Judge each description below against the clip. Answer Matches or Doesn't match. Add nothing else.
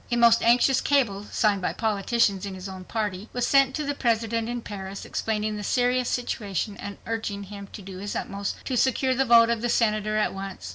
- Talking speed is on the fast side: Matches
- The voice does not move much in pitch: Doesn't match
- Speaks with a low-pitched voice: Doesn't match